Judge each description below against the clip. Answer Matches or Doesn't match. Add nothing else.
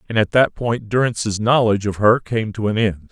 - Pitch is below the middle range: Matches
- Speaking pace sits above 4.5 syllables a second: Matches